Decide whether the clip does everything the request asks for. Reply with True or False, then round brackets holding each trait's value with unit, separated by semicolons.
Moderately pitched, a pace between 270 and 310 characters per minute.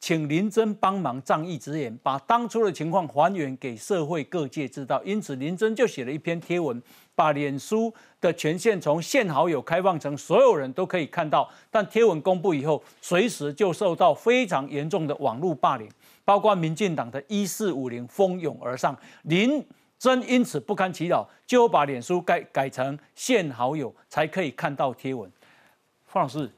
False (170 Hz; 260 characters per minute)